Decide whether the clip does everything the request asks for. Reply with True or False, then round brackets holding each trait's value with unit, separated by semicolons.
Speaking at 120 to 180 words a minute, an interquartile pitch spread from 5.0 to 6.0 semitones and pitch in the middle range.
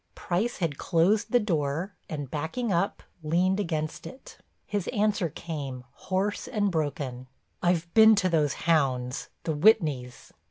True (135 wpm; 5.5 semitones; 170 Hz)